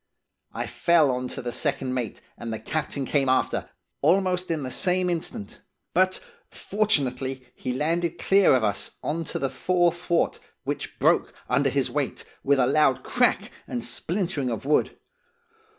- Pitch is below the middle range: No, medium, 145 Hz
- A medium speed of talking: Yes, average, 160 wpm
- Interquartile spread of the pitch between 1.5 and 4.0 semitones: No, average, 5.3 semitones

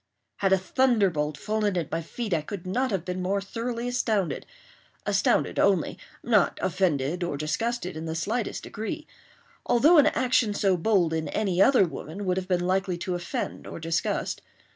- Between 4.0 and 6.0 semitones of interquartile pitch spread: Yes, average, 4.5 semitones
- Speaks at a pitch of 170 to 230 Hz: Yes, high, 190 Hz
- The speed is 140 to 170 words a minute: Yes, average, 165 wpm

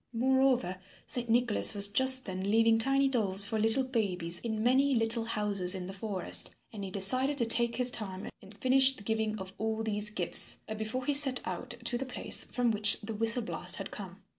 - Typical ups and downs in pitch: Yes, average, 3.7 semitones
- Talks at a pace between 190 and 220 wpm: Yes, average, 200 wpm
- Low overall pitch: No, high, 225 Hz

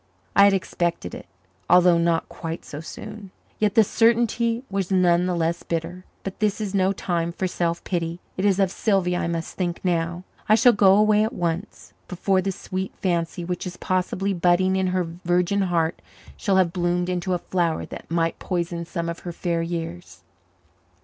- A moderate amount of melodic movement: No, narrow, 2.3 semitones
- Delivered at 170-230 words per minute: Yes, average, 185 wpm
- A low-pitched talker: No, medium, 180 Hz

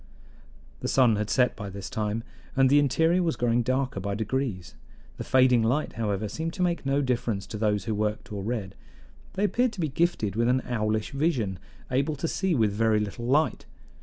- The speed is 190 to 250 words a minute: Yes, average, 195 wpm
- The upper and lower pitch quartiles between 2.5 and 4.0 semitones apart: No, average, 4.9 semitones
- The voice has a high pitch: No, low, 120 Hz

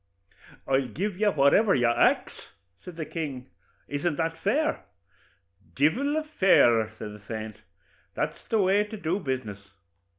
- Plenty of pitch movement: Yes, wide, 8.2 semitones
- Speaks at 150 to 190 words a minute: No, average, 140 wpm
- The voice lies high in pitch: No, medium, 160 Hz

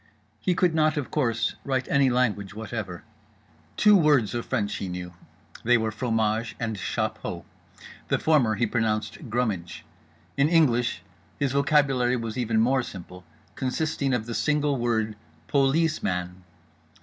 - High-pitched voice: No, low, 120 Hz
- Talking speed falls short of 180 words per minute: Yes, average, 145 wpm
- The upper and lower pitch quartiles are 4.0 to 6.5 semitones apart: Yes, average, 4.4 semitones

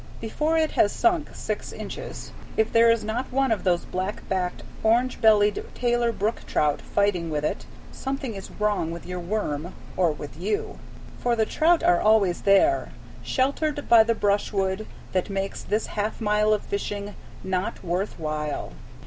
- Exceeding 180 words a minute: No, average, 165 wpm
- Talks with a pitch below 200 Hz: No, high, 210 Hz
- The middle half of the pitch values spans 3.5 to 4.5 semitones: Yes, average, 3.9 semitones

